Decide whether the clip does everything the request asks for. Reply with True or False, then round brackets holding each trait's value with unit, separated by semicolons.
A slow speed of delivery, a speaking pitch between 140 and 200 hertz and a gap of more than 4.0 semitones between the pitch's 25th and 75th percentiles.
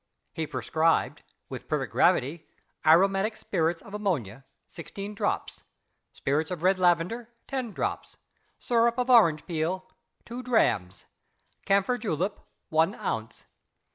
True (115 wpm; 185 Hz; 5.2 semitones)